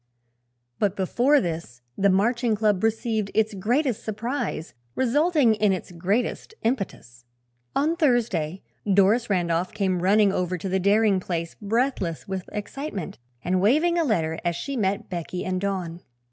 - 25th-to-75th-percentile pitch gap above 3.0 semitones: Yes, average, 4.5 semitones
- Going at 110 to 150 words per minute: Yes, average, 145 wpm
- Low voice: No, high, 200 Hz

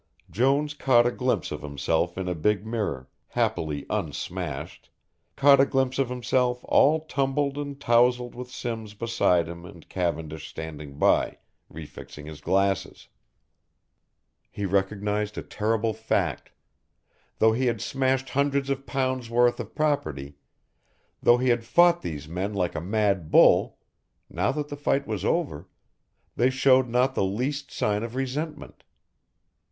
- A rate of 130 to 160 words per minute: Yes, average, 145 wpm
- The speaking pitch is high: No, low, 115 Hz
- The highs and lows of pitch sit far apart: Yes, wide, 6.5 semitones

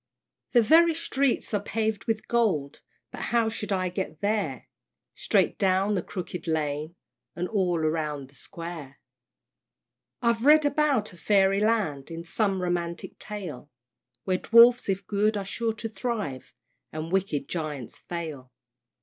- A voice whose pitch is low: No, high, 190 Hz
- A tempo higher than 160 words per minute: No, average, 140 wpm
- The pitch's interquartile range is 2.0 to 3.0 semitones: No, wide, 5.5 semitones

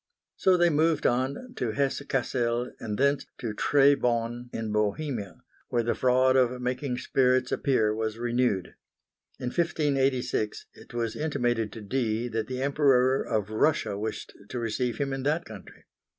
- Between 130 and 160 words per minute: Yes, average, 150 wpm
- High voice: No, low, 125 Hz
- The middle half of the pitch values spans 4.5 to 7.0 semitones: No, average, 3.3 semitones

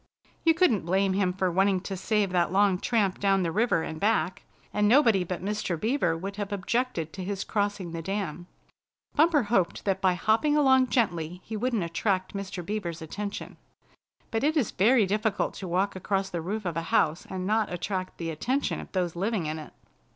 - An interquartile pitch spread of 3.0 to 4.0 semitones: Yes, average, 3.3 semitones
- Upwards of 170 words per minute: Yes, average, 195 wpm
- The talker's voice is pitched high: Yes, high, 195 Hz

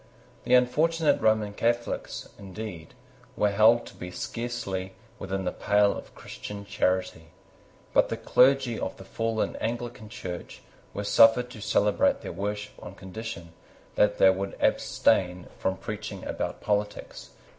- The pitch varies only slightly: No, average, 3.5 semitones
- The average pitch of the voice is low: Yes, low, 105 Hz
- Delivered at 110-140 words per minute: Yes, slow, 135 wpm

